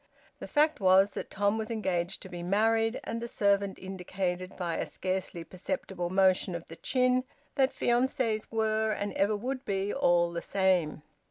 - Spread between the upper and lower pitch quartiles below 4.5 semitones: Yes, average, 3.5 semitones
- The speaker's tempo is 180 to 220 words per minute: No, average, 170 wpm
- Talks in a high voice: Yes, high, 195 Hz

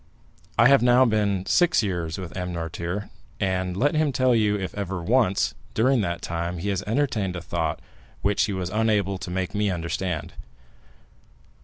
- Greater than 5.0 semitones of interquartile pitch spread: No, average, 4.0 semitones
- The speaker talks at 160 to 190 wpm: Yes, average, 170 wpm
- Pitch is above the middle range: No, very low, 95 Hz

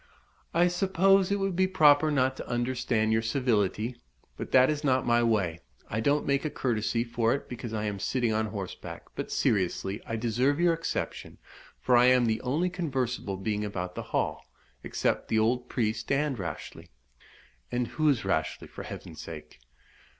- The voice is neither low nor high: No, low, 120 Hz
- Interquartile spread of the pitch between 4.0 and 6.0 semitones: Yes, average, 4.8 semitones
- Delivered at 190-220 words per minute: No, average, 175 wpm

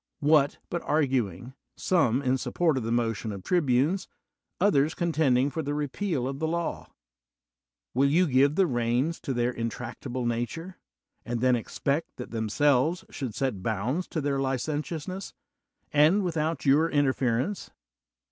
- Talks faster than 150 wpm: No, average, 145 wpm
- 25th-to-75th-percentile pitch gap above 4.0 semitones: Yes, average, 4.6 semitones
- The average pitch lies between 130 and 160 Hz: Yes, medium, 140 Hz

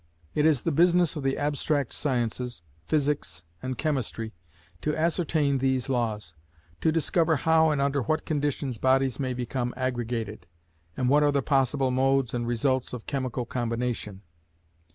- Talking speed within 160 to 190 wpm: No, average, 150 wpm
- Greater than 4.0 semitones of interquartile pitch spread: No, average, 3.4 semitones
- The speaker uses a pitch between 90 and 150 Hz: Yes, low, 135 Hz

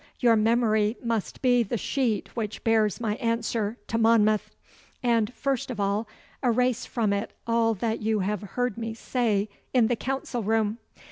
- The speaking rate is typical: Yes, average, 160 wpm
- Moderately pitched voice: No, high, 225 Hz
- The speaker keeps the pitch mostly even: Yes, narrow, 2.0 semitones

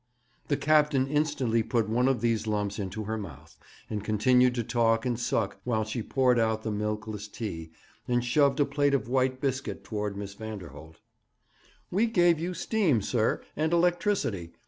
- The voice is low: Yes, low, 120 Hz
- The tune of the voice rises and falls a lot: No, average, 4.6 semitones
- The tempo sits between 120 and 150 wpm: No, average, 170 wpm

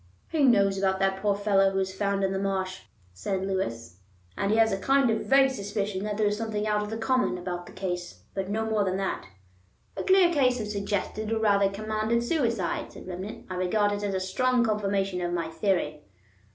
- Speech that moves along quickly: Yes, fast, 215 wpm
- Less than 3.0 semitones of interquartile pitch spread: Yes, narrow, 2.5 semitones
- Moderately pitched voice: No, high, 200 Hz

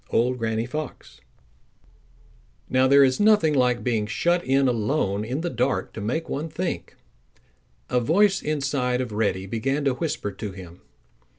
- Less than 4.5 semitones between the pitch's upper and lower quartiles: No, average, 5.1 semitones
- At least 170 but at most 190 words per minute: No, average, 155 wpm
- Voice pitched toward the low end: Yes, low, 130 Hz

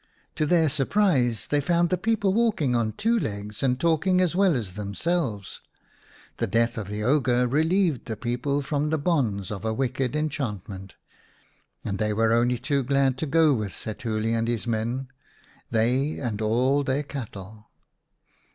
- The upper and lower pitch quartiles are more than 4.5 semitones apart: Yes, wide, 5.5 semitones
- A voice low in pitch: Yes, low, 125 Hz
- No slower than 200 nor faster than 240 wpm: No, average, 160 wpm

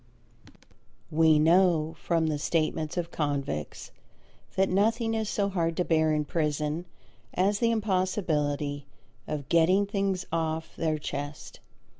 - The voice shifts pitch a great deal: No, average, 3.7 semitones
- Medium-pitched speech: Yes, medium, 165 Hz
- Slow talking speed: Yes, slow, 125 wpm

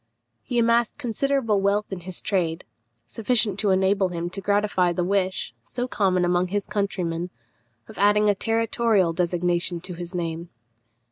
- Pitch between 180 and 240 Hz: Yes, high, 190 Hz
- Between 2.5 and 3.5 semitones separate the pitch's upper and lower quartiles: Yes, average, 3.0 semitones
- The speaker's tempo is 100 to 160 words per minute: Yes, average, 150 wpm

